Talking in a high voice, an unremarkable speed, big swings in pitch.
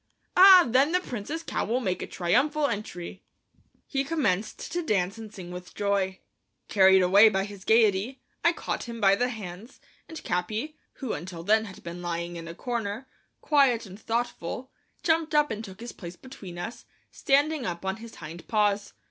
Yes: high, 215 Hz; average, 180 wpm; wide, 5.8 semitones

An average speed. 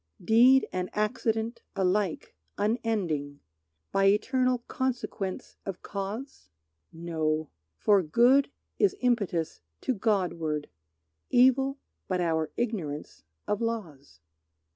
No: slow, 95 wpm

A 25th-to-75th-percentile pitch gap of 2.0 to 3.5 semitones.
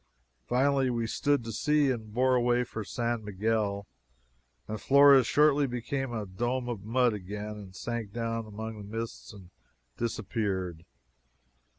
Yes: average, 3.1 semitones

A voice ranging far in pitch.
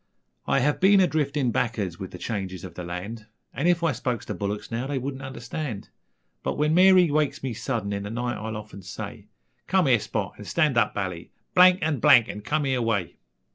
Yes: wide, 6.3 semitones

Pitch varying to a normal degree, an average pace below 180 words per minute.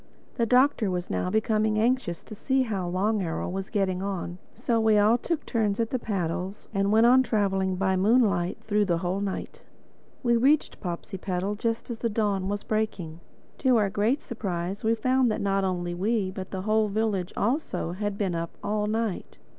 No: average, 3.2 semitones; average, 185 wpm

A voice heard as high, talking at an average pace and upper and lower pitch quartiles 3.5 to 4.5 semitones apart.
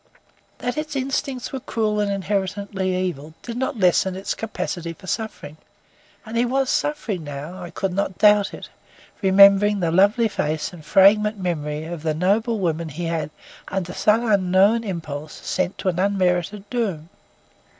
Yes: high, 195 Hz; average, 160 wpm; average, 3.8 semitones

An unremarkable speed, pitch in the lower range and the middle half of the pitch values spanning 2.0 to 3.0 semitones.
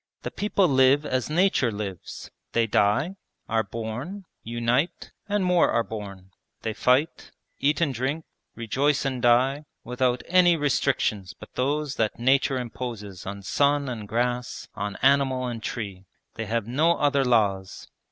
No: average, 145 wpm; low, 125 Hz; average, 4.3 semitones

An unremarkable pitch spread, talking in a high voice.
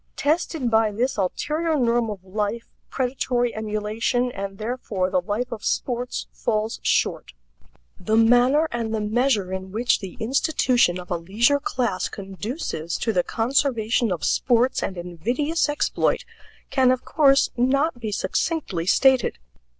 Yes: average, 4.2 semitones; high, 230 Hz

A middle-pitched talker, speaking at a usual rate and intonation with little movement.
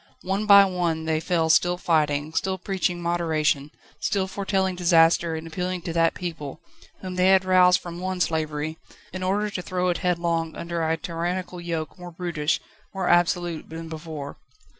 Yes: medium, 175 Hz; average, 165 wpm; narrow, 2.1 semitones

